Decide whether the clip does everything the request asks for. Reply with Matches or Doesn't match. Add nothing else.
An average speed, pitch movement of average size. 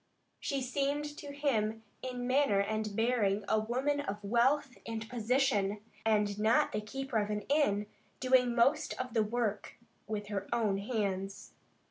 Matches